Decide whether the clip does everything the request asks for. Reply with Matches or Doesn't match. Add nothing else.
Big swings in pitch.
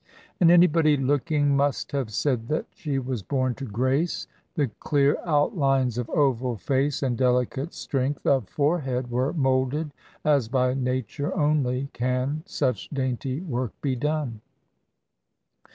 Doesn't match